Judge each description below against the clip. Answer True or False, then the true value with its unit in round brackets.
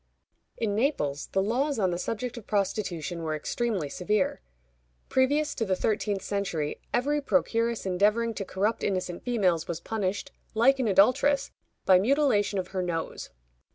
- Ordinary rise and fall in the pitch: True (4.5 semitones)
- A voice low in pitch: False (205 Hz)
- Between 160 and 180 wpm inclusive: False (150 wpm)